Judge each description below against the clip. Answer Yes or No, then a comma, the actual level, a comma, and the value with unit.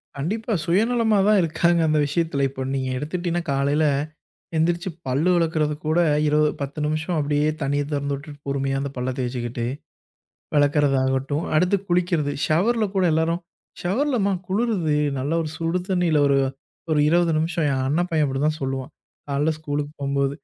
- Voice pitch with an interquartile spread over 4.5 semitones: No, average, 3.7 semitones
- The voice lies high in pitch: No, medium, 155 Hz